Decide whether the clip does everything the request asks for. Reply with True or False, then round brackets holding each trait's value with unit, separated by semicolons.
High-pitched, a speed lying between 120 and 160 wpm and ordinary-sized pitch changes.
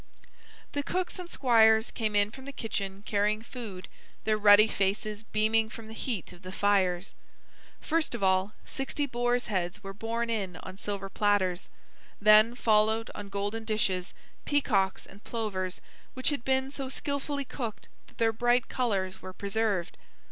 True (215 Hz; 155 wpm; 3.5 semitones)